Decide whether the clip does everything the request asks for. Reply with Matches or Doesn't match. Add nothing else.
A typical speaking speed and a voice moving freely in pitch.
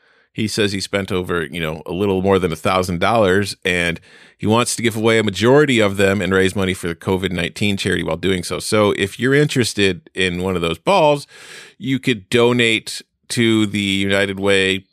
Doesn't match